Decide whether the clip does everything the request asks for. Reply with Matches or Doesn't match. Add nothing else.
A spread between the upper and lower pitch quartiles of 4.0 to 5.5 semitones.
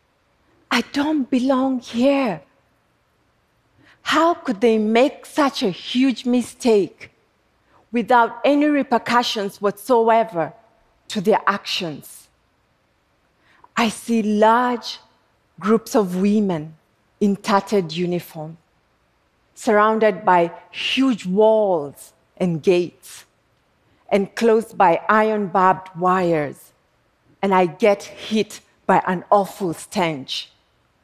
Matches